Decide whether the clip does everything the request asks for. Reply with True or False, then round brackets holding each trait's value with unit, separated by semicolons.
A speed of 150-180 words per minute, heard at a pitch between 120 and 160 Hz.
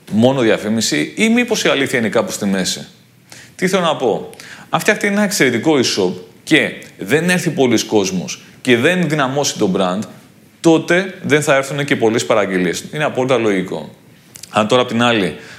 True (170 wpm; 140 Hz)